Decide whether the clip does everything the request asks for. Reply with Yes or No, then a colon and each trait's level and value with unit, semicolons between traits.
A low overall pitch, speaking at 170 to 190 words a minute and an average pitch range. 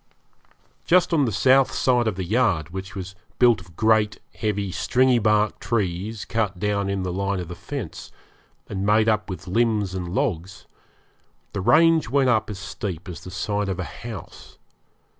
Yes: low, 105 Hz; average, 175 wpm; average, 3.4 semitones